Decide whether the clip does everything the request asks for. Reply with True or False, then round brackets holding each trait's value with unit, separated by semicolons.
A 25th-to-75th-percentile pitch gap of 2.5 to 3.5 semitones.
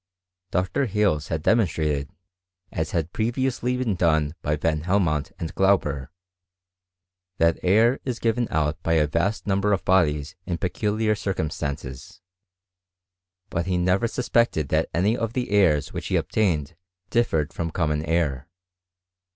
False (5.4 semitones)